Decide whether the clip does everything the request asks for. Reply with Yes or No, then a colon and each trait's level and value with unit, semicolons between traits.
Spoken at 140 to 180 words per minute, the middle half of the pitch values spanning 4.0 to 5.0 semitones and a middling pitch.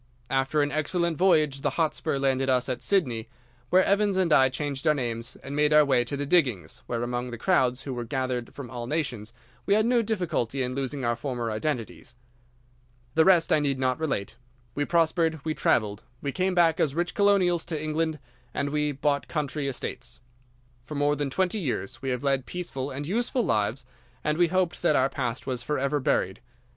No: average, 195 wpm; average, 4.3 semitones; medium, 145 Hz